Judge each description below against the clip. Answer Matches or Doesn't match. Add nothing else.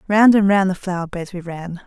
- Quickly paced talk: Matches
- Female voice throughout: Matches